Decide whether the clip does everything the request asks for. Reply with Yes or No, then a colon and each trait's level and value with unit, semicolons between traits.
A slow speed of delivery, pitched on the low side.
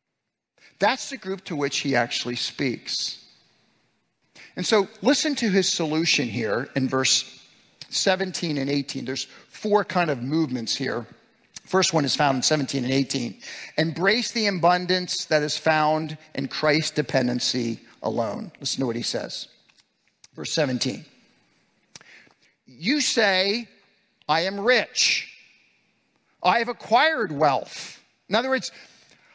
No: slow, 130 wpm; medium, 160 Hz